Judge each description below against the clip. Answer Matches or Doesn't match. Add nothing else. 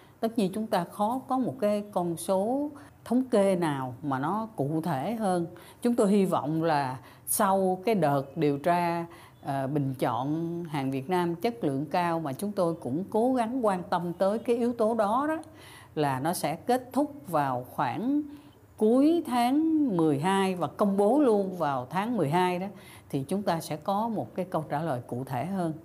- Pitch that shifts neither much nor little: Doesn't match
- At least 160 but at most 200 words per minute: Matches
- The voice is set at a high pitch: Doesn't match